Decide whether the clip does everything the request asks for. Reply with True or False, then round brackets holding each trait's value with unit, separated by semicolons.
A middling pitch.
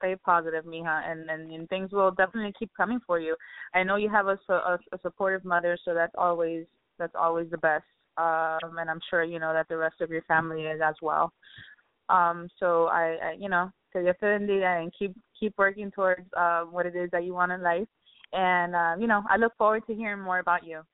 True (175 Hz)